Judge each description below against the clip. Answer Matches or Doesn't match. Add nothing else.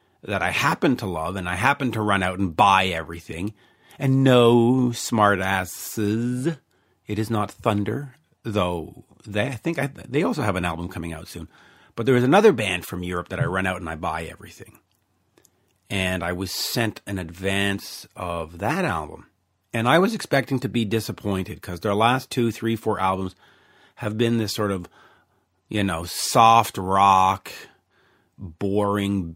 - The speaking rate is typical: Matches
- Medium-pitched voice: Doesn't match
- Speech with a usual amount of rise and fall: Matches